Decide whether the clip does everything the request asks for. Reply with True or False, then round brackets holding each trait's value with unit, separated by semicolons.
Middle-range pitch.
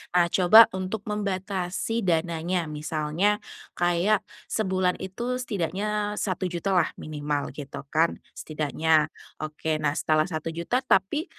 True (180 Hz)